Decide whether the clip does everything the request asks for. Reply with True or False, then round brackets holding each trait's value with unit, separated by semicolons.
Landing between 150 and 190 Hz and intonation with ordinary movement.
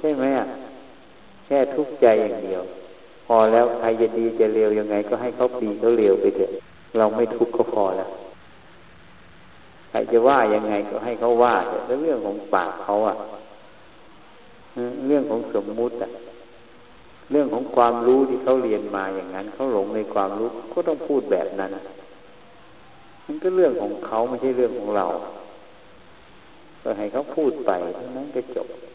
False (120 Hz; 3.8 semitones)